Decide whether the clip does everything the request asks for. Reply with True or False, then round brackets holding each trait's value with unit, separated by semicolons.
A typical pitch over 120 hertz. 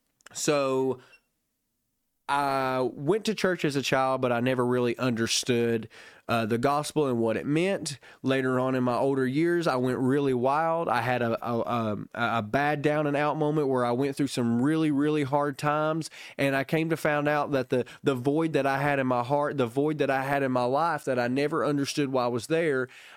True (135 Hz)